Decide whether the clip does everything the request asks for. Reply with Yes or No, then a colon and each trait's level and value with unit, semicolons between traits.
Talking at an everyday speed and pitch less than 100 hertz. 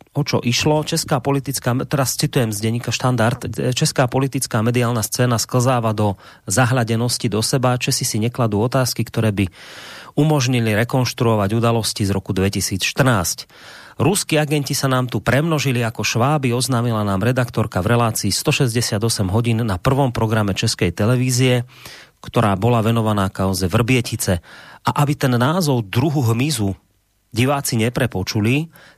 No: average, 135 wpm; low, 120 Hz